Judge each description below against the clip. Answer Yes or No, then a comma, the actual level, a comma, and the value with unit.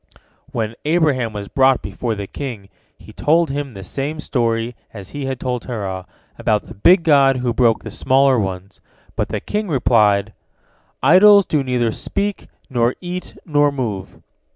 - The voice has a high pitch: No, low, 125 Hz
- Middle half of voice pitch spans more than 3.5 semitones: Yes, average, 5.1 semitones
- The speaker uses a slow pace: No, average, 160 wpm